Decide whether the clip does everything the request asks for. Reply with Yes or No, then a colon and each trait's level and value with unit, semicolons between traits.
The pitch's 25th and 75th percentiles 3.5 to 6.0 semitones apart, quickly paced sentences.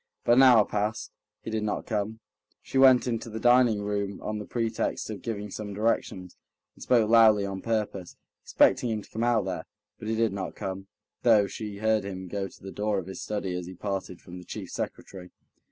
No: narrow, 2.5 semitones; fast, 210 wpm